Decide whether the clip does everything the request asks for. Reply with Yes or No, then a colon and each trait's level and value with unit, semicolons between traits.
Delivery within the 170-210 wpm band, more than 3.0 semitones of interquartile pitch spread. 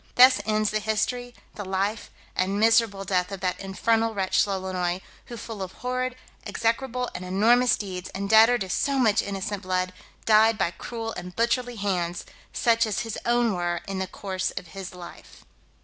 Yes: average, 175 wpm; average, 3.5 semitones